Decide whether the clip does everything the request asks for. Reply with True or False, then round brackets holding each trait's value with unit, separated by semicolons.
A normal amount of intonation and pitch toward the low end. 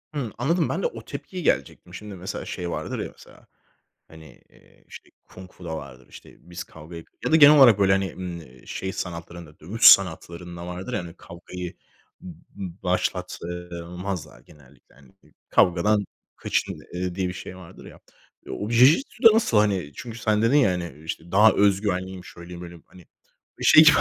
True (3.4 semitones; 90 Hz)